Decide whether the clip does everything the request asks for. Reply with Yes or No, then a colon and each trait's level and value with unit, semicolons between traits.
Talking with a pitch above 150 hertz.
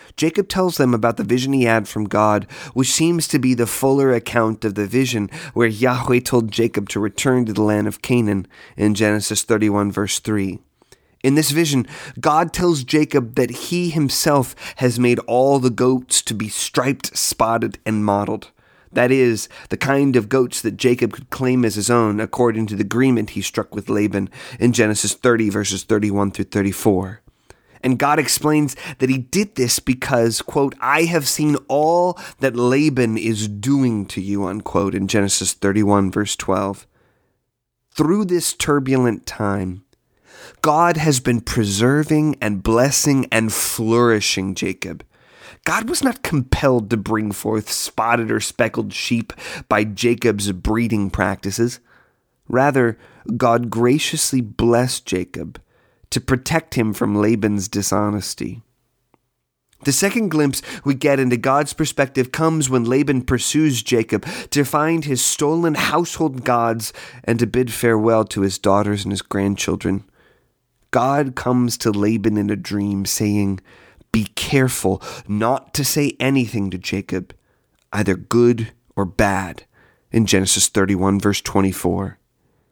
No: low, 120 Hz